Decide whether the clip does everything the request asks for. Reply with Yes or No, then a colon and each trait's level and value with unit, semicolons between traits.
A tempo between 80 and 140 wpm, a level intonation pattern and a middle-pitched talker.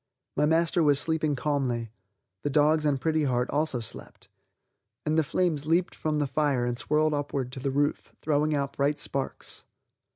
No: average, 170 wpm; narrow, 2.1 semitones; medium, 145 Hz